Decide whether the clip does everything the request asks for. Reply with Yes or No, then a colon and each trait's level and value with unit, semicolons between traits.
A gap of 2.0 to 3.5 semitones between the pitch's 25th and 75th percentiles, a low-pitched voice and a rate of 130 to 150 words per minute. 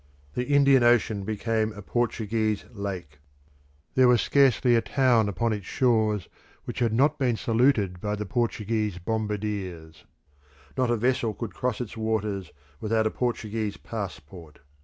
Yes: average, 2.9 semitones; low, 110 Hz; average, 140 wpm